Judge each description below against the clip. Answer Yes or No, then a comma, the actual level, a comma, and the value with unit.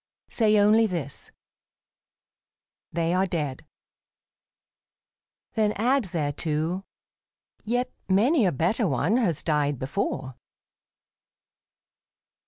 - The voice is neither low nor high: Yes, medium, 180 Hz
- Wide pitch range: Yes, wide, 6.4 semitones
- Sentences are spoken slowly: Yes, slow, 90 wpm